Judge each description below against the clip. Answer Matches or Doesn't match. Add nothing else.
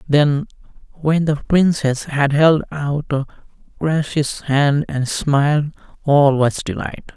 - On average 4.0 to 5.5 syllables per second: Doesn't match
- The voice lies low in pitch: Doesn't match